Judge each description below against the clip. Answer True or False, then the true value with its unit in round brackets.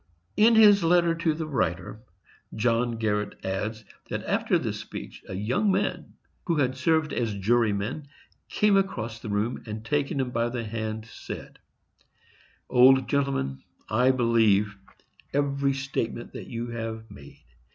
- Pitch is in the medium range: False (120 Hz)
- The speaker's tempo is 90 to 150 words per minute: True (140 wpm)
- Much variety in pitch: False (4.5 semitones)